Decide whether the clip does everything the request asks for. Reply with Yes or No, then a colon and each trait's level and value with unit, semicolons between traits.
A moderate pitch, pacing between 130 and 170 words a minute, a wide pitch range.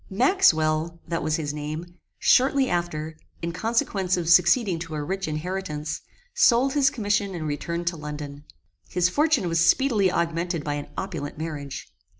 No: medium, 170 Hz; average, 155 wpm; average, 4.1 semitones